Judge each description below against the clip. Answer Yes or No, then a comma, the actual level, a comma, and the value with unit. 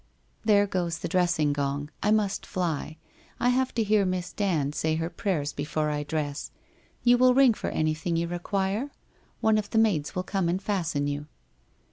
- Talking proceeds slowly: No, average, 185 wpm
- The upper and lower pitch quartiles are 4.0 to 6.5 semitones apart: Yes, average, 5.2 semitones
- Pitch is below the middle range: No, medium, 175 Hz